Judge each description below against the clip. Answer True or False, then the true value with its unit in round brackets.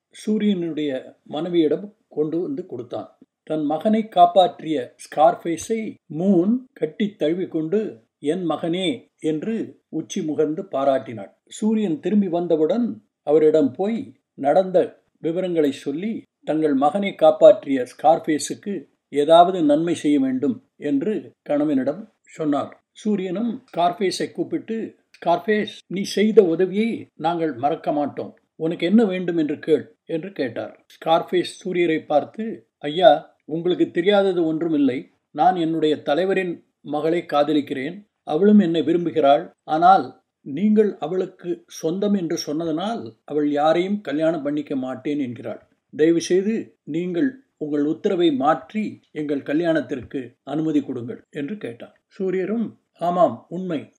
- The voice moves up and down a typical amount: False (5.8 semitones)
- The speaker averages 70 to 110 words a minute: True (105 wpm)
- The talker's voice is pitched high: False (175 Hz)